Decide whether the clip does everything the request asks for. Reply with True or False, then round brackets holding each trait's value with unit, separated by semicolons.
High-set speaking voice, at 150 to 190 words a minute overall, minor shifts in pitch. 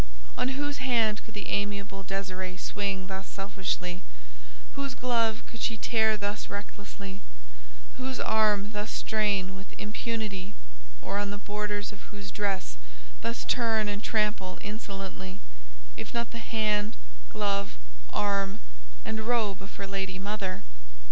False (205 Hz; 135 wpm; 2.0 semitones)